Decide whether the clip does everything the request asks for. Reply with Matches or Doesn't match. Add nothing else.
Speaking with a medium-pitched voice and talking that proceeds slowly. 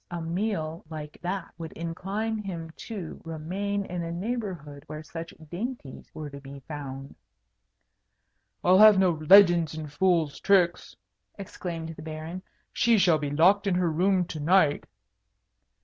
Doesn't match